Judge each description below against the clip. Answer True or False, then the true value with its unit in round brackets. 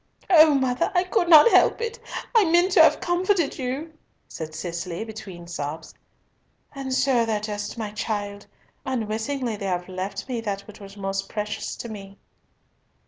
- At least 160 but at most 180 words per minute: True (165 wpm)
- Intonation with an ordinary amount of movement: False (6.0 semitones)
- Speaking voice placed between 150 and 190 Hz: False (220 Hz)